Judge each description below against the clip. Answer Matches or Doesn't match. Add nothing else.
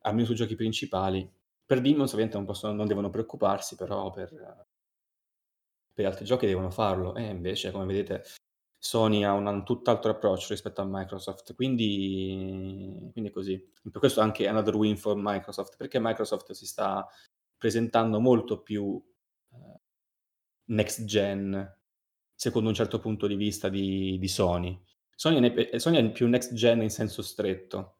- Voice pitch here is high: Doesn't match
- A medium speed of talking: Matches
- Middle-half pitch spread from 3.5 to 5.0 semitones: Doesn't match